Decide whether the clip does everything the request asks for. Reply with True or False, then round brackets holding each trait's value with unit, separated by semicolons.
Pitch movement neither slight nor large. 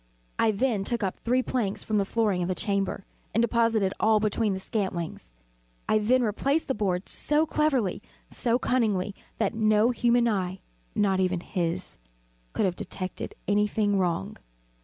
True (3.6 semitones)